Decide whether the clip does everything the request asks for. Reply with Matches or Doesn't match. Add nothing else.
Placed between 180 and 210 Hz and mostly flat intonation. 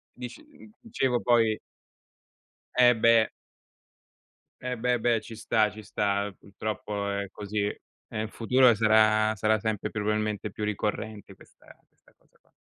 Doesn't match